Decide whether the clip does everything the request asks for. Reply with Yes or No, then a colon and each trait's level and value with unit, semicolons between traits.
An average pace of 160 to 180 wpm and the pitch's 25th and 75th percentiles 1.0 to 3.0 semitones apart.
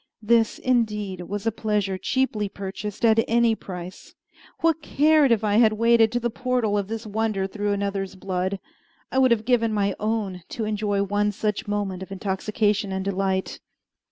Yes: average, 175 wpm; narrow, 2.5 semitones